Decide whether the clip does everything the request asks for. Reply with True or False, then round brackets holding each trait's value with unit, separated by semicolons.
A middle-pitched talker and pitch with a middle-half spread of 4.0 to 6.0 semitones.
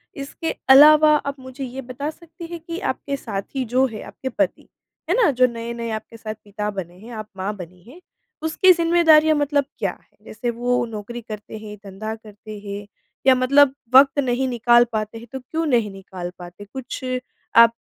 False (245 Hz; 4.7 semitones)